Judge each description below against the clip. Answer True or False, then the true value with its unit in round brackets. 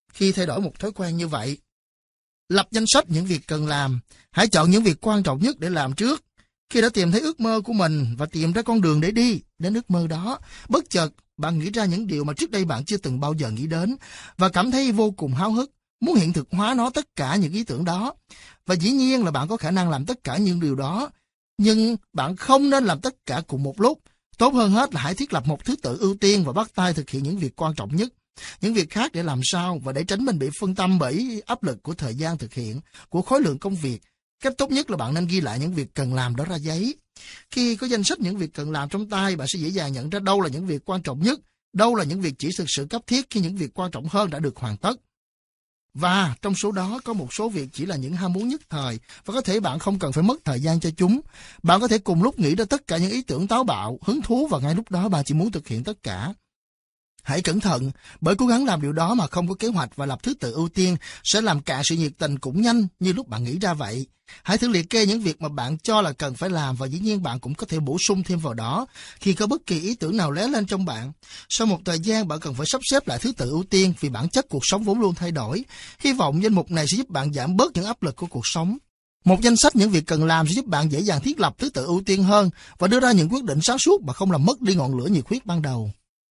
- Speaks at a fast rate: True (285 wpm)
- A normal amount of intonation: False (6.1 semitones)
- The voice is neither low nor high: True (180 Hz)